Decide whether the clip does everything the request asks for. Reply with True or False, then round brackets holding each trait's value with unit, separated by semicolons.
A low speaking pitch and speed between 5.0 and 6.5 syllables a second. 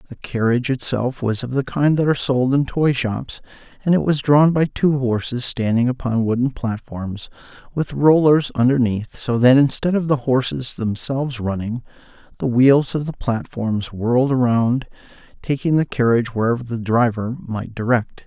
False (125 Hz; 4.8 syllables/s)